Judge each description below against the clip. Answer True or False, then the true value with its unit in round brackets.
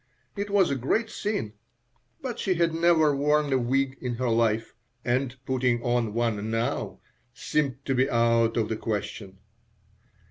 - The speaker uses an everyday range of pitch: True (4.4 semitones)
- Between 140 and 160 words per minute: True (155 wpm)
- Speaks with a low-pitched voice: True (130 Hz)